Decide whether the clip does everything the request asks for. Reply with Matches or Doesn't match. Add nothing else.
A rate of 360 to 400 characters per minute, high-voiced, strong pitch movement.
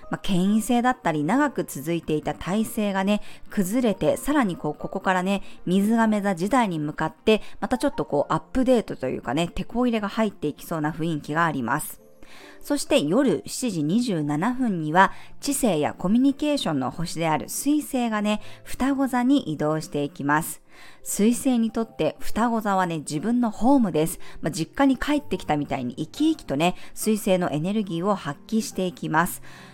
Matches